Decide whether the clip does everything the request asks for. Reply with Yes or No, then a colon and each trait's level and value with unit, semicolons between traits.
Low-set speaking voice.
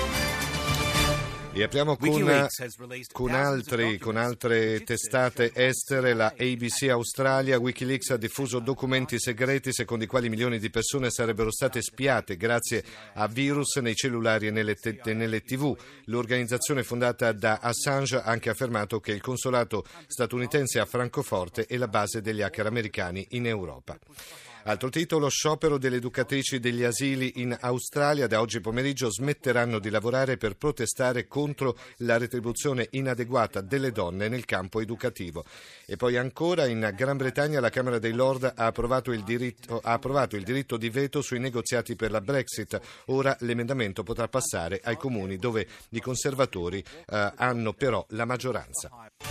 Yes: low, 125 Hz